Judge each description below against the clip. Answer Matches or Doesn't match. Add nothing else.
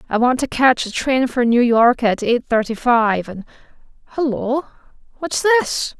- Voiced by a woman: Matches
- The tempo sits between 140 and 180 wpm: Matches